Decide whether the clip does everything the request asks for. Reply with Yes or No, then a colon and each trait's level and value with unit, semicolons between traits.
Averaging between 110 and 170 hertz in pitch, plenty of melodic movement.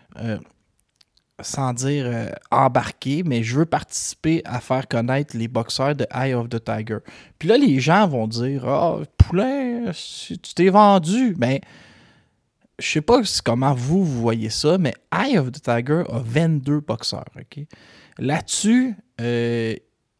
Yes: low, 135 Hz; wide, 6.0 semitones